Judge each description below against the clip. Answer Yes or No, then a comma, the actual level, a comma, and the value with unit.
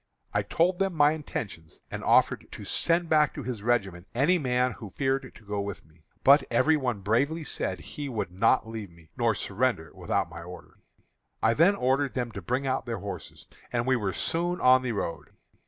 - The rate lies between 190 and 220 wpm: Yes, average, 200 wpm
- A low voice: Yes, low, 125 Hz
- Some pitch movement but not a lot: No, wide, 6.2 semitones